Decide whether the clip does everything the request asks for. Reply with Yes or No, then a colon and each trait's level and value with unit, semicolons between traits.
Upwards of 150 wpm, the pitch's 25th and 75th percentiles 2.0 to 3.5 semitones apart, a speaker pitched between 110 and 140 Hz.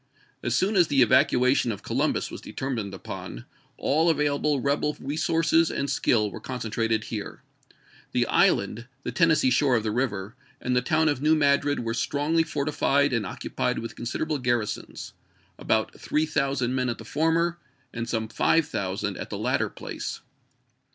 No: average, 160 wpm; average, 4.7 semitones; low, 135 Hz